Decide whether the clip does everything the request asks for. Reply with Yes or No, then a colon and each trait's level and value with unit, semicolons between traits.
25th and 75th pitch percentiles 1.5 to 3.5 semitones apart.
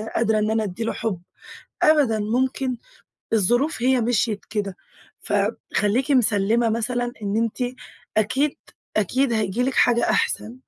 Yes: average, 2.9 semitones